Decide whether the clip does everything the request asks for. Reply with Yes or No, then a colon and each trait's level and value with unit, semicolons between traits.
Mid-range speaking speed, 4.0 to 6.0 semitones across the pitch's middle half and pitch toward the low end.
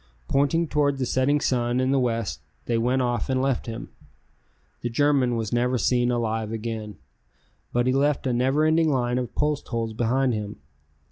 No: average, 180 wpm; average, 2.7 semitones; low, 125 Hz